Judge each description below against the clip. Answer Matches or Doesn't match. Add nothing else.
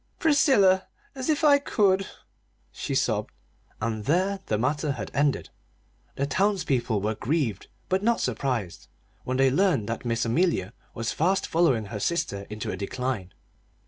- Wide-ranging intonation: Matches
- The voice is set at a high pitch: Doesn't match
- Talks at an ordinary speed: Matches